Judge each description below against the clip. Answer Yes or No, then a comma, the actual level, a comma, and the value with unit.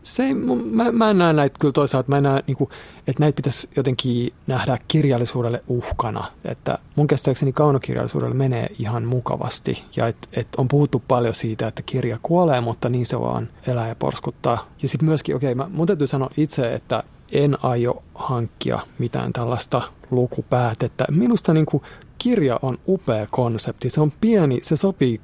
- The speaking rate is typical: No, fast, 175 wpm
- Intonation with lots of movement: No, average, 3.6 semitones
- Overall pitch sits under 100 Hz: No, low, 135 Hz